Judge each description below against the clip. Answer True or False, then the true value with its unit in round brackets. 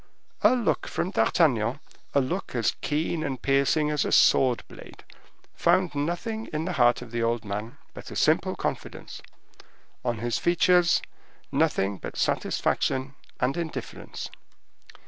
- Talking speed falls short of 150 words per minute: True (135 wpm)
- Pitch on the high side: False (140 Hz)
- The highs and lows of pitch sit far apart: True (6.1 semitones)